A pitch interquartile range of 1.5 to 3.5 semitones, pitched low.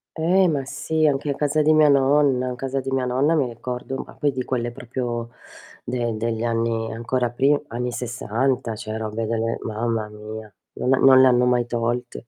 Yes: average, 2.7 semitones; low, 125 Hz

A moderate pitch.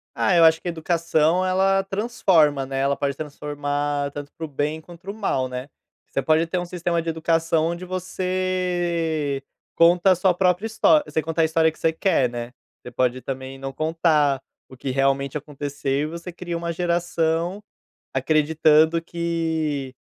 Yes: medium, 160 Hz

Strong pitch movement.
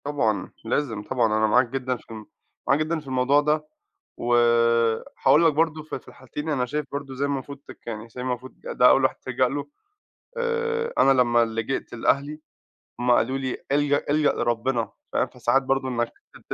No: average, 3.4 semitones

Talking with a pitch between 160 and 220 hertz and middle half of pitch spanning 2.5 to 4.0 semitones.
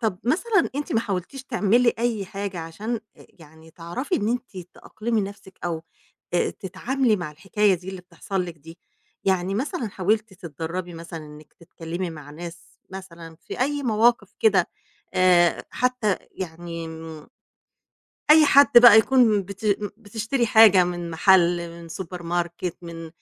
No: high, 190 Hz; average, 4.7 semitones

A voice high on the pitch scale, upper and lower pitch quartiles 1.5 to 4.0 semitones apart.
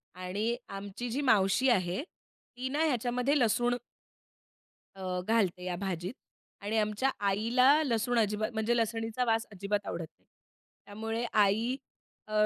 Yes: high, 220 Hz; average, 3.5 semitones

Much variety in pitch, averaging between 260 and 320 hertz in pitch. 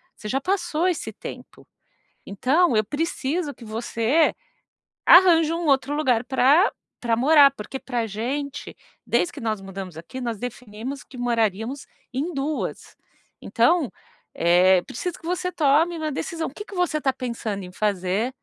Yes: wide, 6.1 semitones; very high, 265 Hz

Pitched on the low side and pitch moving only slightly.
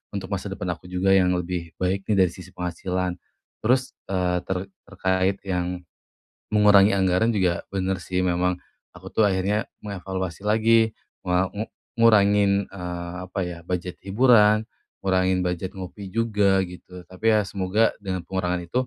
Yes: very low, 95 Hz; narrow, 2.1 semitones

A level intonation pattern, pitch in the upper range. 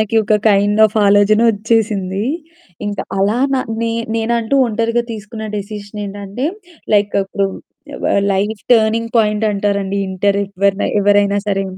Yes: narrow, 1.7 semitones; high, 205 Hz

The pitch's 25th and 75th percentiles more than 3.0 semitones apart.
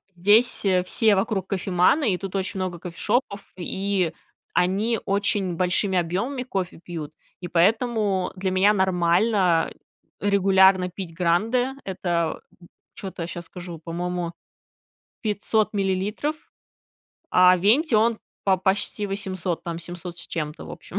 No: narrow, 2.5 semitones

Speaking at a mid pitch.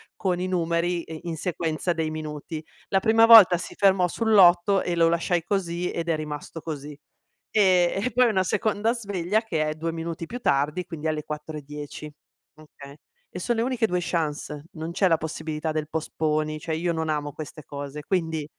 Yes: medium, 165 Hz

